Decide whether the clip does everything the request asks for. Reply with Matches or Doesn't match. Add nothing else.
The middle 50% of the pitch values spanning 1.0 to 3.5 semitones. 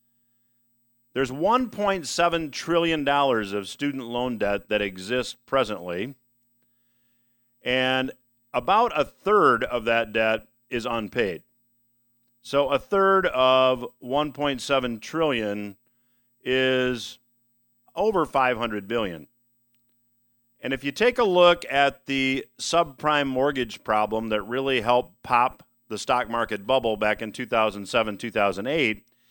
Matches